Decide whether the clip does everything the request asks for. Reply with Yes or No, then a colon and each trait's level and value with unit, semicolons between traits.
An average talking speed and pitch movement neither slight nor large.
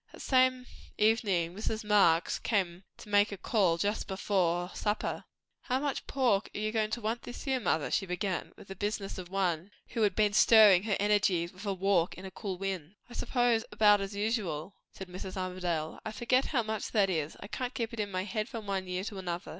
No: fast, 215 wpm; average, 3.0 semitones